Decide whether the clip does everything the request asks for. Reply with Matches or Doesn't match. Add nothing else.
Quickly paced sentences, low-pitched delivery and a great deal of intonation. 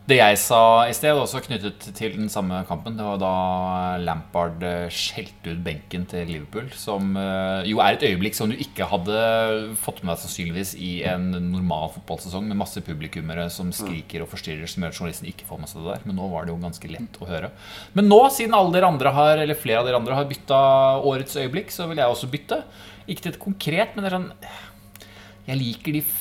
Matches